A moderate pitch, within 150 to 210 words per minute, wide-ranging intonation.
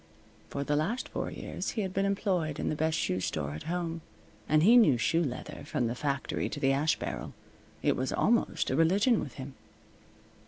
Yes: medium, 155 Hz; average, 200 wpm; wide, 5.9 semitones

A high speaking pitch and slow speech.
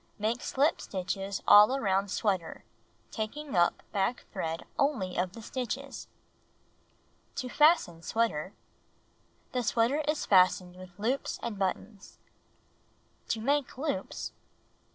Yes: high, 215 Hz; slow, 115 wpm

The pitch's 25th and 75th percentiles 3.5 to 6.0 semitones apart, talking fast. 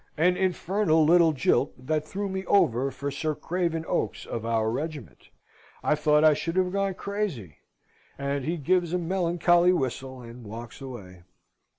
No: wide, 5.5 semitones; average, 160 wpm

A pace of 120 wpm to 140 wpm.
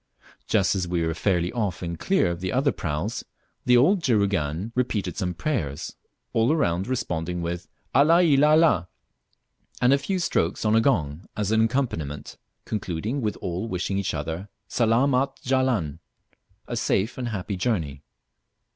No: average, 155 wpm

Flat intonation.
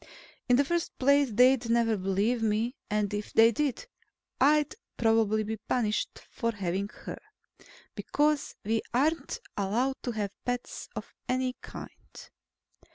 No: average, 4.0 semitones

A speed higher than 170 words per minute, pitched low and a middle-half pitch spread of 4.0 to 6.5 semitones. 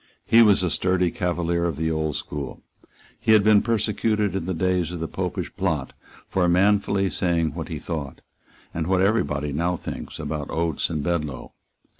No: average, 180 wpm; very low, 85 Hz; average, 3.3 semitones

